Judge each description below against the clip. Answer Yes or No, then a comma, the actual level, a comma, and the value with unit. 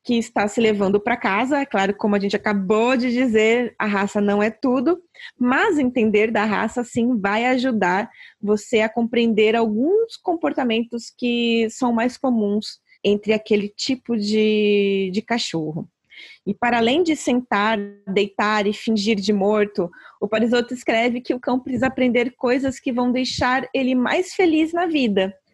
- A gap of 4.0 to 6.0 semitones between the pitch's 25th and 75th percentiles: No, average, 3.4 semitones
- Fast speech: No, average, 160 wpm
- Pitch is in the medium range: No, high, 230 Hz